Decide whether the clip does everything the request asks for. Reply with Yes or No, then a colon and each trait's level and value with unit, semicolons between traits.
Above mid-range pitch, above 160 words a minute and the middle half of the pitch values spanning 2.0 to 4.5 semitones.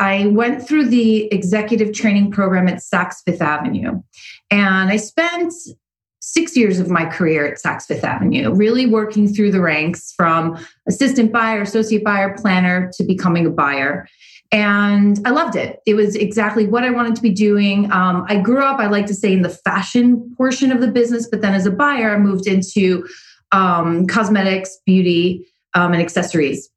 Yes: high, 205 Hz; average, 180 wpm; average, 3.5 semitones